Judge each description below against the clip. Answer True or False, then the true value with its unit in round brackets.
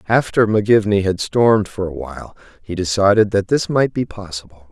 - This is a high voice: False (105 Hz)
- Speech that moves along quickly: False (180 wpm)